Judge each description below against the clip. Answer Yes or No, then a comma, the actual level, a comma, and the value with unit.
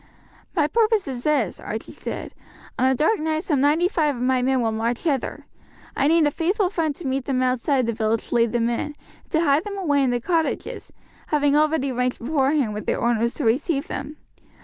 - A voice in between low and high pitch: No, very high, 280 Hz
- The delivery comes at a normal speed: No, fast, 215 wpm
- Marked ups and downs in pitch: No, average, 4.2 semitones